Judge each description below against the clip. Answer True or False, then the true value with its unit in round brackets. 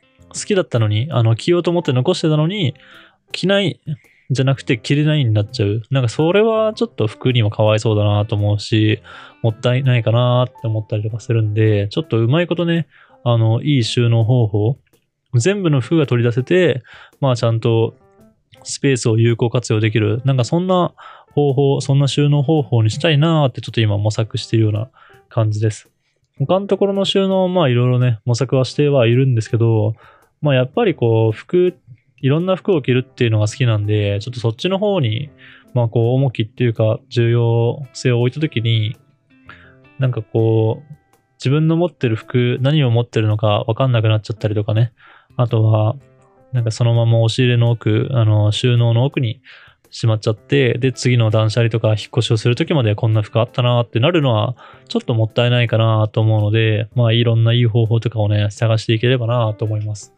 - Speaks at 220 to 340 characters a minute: False (395 characters per minute)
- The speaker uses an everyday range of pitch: True (3.7 semitones)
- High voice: False (120 Hz)